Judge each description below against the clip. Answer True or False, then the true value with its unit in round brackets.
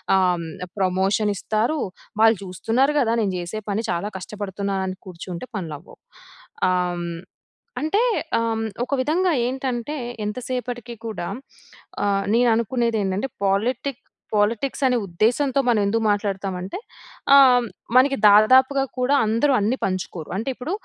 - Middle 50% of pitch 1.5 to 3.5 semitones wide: False (4.9 semitones)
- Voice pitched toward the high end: True (215 Hz)